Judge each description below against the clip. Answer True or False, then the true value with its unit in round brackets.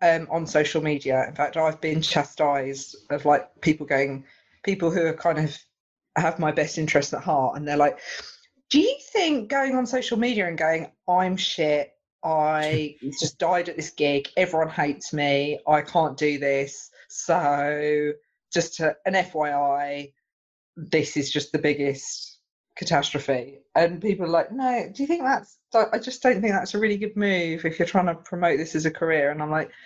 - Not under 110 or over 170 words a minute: False (185 wpm)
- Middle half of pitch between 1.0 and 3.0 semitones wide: False (3.9 semitones)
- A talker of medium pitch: True (160 Hz)